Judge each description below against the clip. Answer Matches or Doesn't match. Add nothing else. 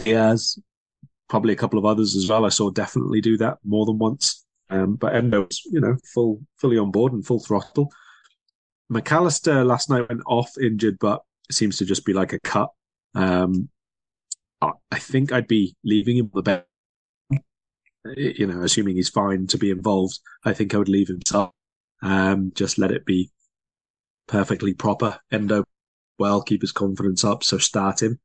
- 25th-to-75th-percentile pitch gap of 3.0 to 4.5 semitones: Matches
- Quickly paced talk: Doesn't match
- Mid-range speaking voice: Doesn't match